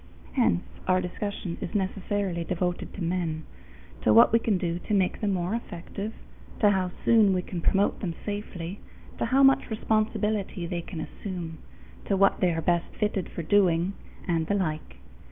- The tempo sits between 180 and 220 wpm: No, average, 170 wpm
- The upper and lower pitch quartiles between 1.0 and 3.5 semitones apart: Yes, average, 3.0 semitones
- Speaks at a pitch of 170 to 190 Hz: Yes, medium, 185 Hz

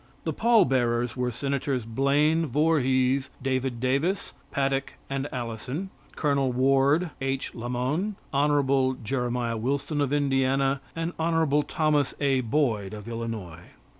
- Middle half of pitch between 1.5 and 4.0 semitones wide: Yes, average, 2.9 semitones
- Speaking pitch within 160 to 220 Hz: No, low, 135 Hz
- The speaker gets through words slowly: Yes, slow, 120 wpm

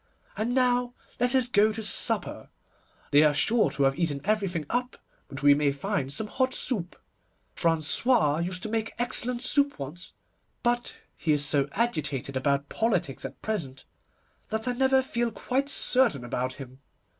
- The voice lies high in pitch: Yes, high, 200 Hz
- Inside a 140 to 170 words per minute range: Yes, average, 160 wpm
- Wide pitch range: Yes, wide, 9.0 semitones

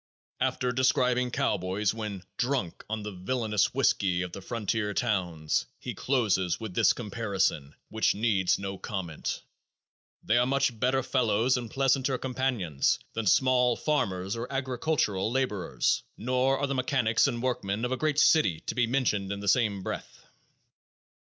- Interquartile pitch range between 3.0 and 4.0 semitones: No, average, 4.7 semitones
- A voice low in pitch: Yes, low, 115 Hz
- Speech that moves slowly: No, average, 150 wpm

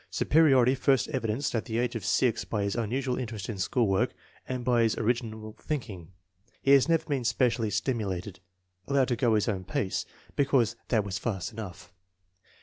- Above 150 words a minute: Yes, average, 175 wpm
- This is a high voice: No, low, 115 Hz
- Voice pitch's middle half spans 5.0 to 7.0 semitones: No, average, 3.6 semitones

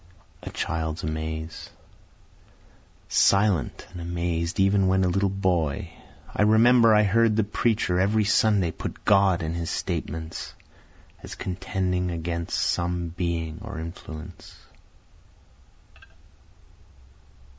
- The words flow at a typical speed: No, slow, 105 wpm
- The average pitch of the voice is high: No, very low, 90 Hz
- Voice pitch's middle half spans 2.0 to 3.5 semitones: Yes, average, 3.1 semitones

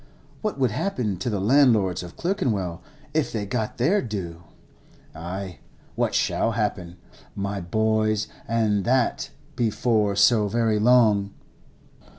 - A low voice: Yes, low, 110 Hz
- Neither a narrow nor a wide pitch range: Yes, average, 3.3 semitones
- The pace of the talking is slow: Yes, slow, 125 wpm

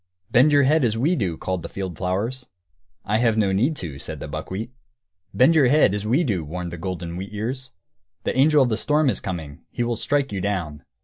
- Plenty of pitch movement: Yes, wide, 6.2 semitones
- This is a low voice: Yes, low, 110 Hz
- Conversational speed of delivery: No, fast, 225 wpm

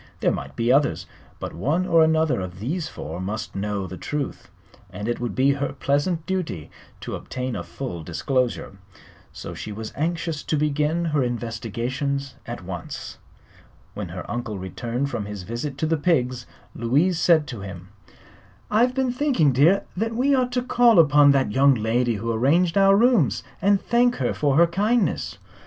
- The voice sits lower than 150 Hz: Yes, medium, 140 Hz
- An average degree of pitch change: No, wide, 6.6 semitones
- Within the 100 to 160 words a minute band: No, average, 175 wpm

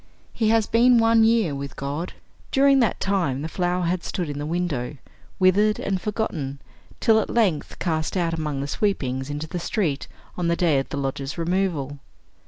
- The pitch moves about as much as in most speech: No, wide, 6.3 semitones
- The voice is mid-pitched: Yes, medium, 170 Hz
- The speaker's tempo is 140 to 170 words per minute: No, average, 185 wpm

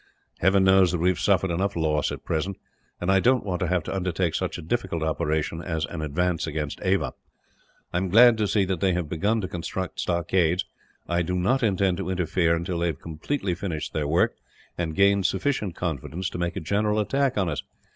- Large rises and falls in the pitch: No, average, 2.7 semitones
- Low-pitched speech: Yes, very low, 90 Hz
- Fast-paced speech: Yes, fast, 210 wpm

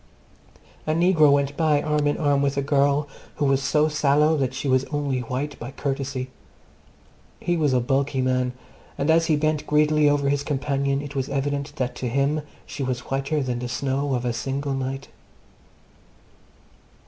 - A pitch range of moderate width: No, narrow, 1.8 semitones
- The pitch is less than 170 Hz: Yes, medium, 140 Hz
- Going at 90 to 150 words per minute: No, average, 175 wpm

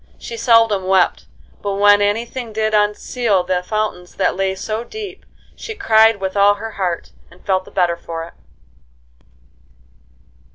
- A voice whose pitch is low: No, high, 205 Hz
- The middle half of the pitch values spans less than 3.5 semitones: Yes, average, 3.0 semitones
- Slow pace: No, average, 155 wpm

